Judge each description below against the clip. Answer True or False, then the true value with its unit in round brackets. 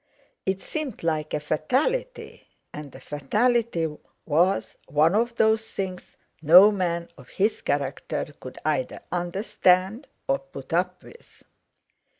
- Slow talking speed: True (125 wpm)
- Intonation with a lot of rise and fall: True (6.1 semitones)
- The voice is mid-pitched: True (180 Hz)